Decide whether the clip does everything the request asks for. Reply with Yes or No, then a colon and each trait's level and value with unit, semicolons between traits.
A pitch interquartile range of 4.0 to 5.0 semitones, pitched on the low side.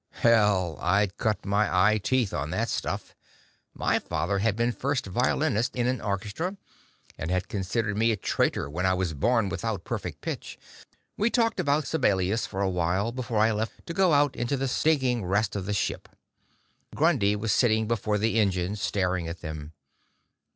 Yes: average, 4.5 semitones; low, 105 Hz